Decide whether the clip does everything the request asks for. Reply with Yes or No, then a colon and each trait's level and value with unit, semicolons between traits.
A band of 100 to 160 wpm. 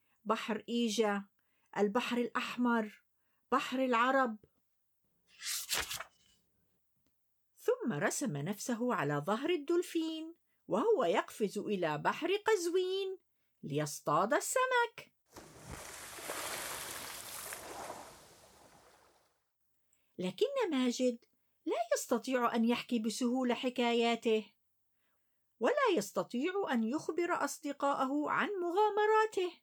No: average, 70 wpm